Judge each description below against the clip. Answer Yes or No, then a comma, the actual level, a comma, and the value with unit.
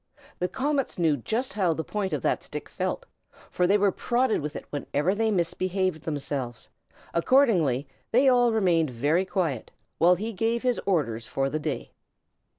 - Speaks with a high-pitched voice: No, medium, 180 Hz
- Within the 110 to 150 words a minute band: No, average, 165 wpm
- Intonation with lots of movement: Yes, wide, 6.8 semitones